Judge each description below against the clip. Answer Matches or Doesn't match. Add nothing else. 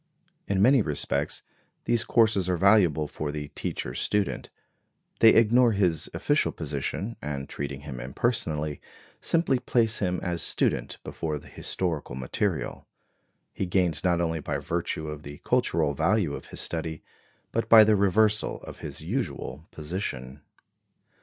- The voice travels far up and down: Matches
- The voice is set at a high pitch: Doesn't match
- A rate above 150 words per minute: Doesn't match